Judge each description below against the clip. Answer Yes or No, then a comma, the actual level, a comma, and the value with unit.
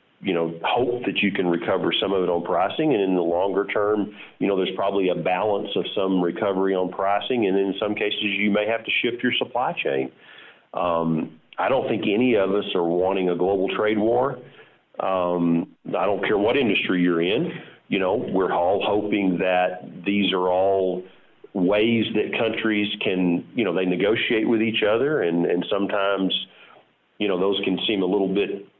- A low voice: Yes, very low, 95 Hz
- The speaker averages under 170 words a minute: No, average, 190 wpm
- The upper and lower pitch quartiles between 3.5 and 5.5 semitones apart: No, average, 2.7 semitones